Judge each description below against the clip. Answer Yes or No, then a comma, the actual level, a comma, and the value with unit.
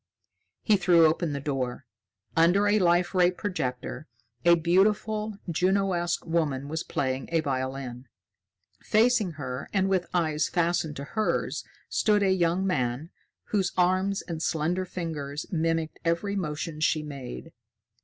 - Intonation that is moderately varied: Yes, average, 3.9 semitones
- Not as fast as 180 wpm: Yes, slow, 135 wpm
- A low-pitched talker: No, medium, 170 Hz